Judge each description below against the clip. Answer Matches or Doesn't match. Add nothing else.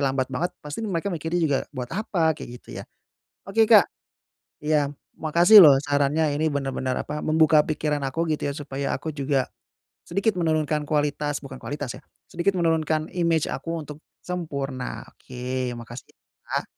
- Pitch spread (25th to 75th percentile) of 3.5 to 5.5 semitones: Doesn't match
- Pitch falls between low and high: Matches